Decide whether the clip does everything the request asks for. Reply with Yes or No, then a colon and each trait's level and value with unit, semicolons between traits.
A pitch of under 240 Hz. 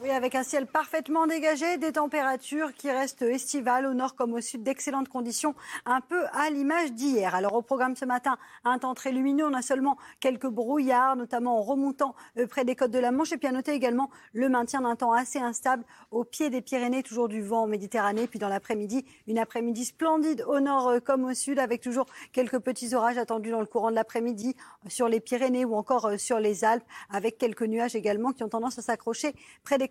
No: very high, 255 Hz